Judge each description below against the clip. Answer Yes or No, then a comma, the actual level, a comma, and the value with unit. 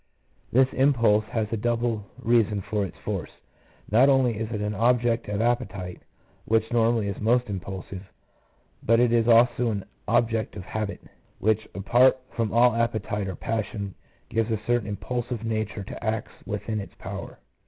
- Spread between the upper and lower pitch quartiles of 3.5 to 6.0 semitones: No, narrow, 2.4 semitones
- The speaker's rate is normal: Yes, average, 160 wpm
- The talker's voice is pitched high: No, low, 110 Hz